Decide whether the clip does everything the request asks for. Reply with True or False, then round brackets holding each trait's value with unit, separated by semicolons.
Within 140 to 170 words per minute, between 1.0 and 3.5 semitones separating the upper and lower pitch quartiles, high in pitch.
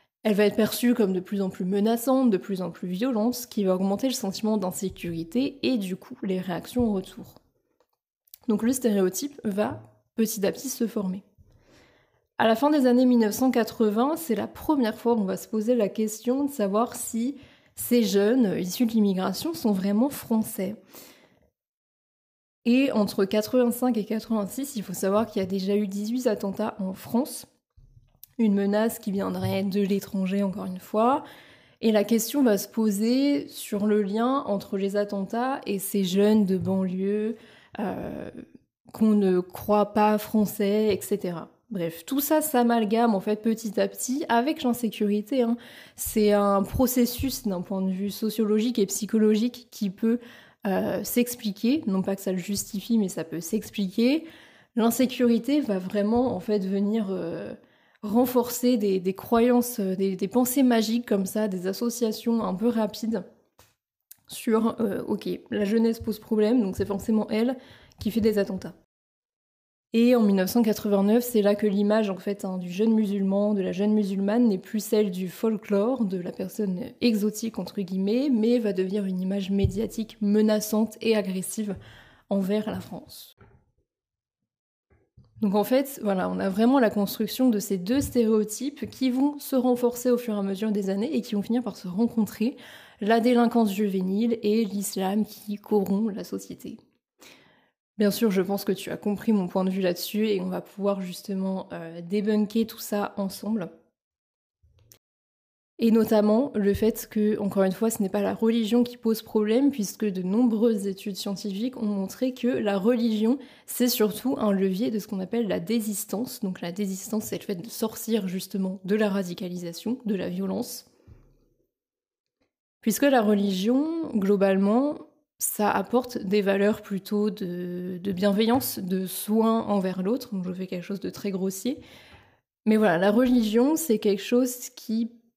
True (165 wpm; 2.9 semitones; 215 Hz)